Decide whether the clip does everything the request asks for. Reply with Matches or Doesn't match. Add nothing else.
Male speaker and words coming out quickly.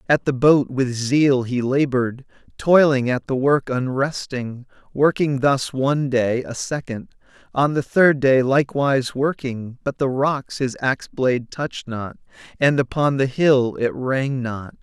Doesn't match